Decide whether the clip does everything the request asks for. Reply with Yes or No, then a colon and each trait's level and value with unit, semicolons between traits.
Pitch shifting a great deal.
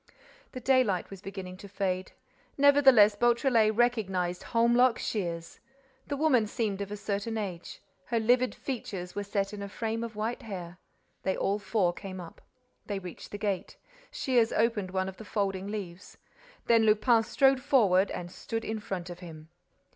No: average, 3.7 semitones